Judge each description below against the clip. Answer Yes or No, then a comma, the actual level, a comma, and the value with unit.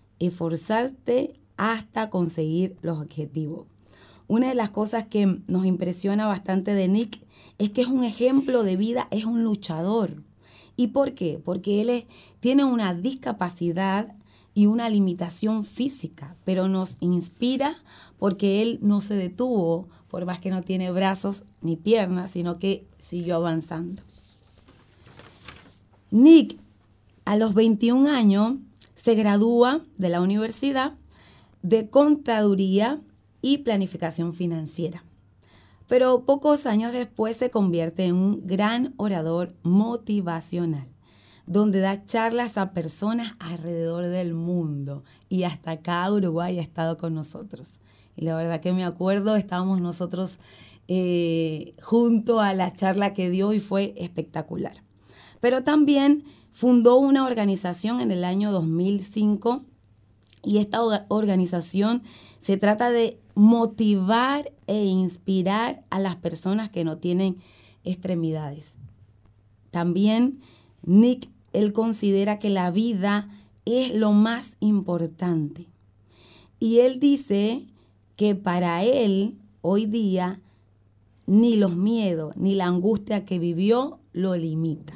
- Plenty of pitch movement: No, average, 4.8 semitones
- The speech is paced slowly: Yes, slow, 120 wpm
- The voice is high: Yes, high, 195 Hz